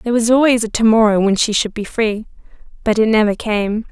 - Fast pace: Yes, fast, 230 wpm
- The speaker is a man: No, female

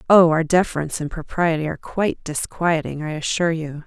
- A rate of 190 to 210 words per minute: No, average, 170 wpm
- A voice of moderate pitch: Yes, medium, 165 Hz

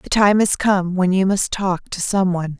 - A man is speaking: No, female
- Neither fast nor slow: No, fast, 255 wpm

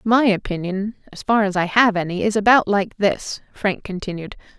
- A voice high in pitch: Yes, high, 200 Hz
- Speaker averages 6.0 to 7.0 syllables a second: No, 5.1 syllables/s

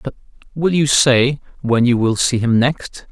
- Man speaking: Yes, male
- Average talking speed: Yes, average, 190 wpm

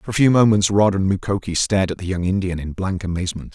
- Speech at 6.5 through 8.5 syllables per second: Yes, 6.6 syllables/s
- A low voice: Yes, very low, 95 Hz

